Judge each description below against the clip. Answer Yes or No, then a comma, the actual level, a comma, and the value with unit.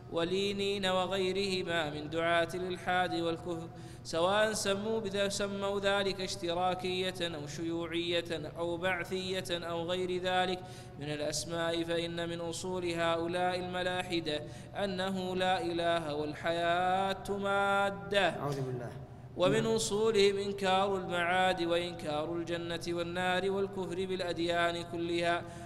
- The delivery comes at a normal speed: Yes, average, 100 wpm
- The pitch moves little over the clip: Yes, narrow, 1.9 semitones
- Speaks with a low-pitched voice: No, medium, 175 Hz